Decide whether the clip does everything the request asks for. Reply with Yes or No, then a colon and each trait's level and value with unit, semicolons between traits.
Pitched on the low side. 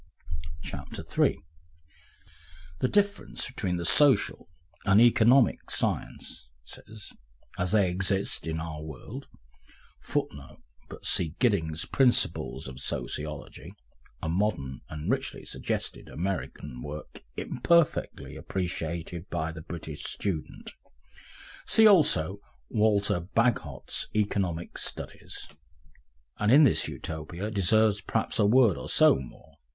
Yes: very low, 90 Hz